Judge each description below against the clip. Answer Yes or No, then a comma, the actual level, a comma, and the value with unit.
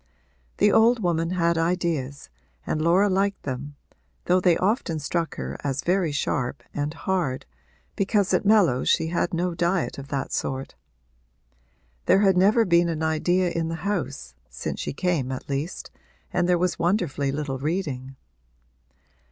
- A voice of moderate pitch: Yes, medium, 170 Hz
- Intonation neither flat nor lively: Yes, average, 4.3 semitones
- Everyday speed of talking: Yes, average, 150 wpm